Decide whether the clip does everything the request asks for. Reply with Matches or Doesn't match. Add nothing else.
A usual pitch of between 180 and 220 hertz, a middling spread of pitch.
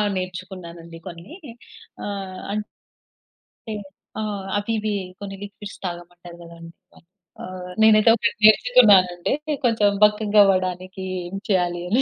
Matches